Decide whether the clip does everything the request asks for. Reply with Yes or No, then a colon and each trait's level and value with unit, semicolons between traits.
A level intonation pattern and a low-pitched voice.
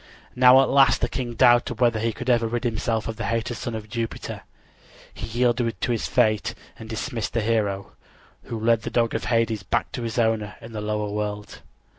Yes: narrow, 1.8 semitones; low, 115 Hz